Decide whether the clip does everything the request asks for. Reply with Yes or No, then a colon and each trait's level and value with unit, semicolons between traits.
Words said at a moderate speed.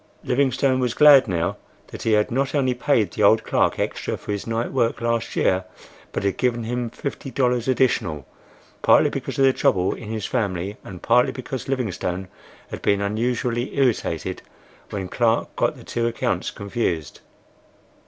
Yes: average, 165 wpm